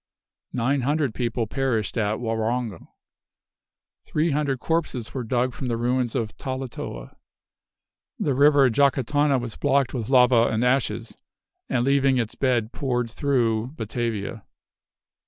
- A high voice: No, low, 125 Hz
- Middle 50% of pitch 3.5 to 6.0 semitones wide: No, average, 3.0 semitones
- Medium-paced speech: No, slow, 125 wpm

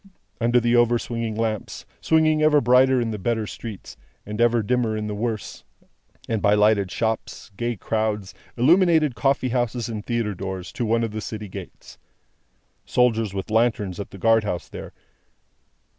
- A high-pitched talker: No, low, 115 Hz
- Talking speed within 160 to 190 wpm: Yes, average, 165 wpm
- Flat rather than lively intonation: Yes, narrow, 2.3 semitones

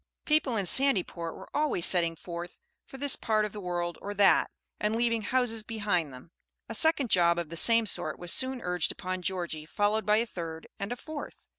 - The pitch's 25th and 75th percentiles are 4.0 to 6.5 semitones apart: Yes, average, 5.0 semitones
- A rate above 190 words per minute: Yes, average, 200 wpm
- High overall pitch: Yes, high, 205 Hz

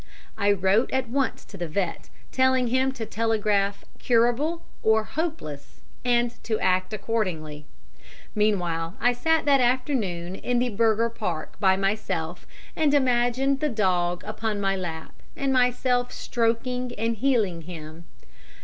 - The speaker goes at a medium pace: No, slow, 130 wpm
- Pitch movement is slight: No, average, 5.0 semitones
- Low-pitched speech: No, high, 220 Hz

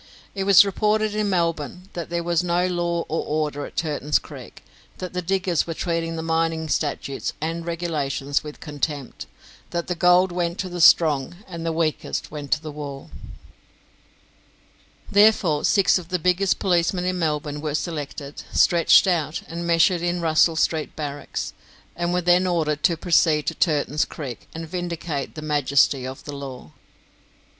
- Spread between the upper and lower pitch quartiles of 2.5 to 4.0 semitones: Yes, average, 2.8 semitones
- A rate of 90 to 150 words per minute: No, average, 165 wpm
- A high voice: No, medium, 165 Hz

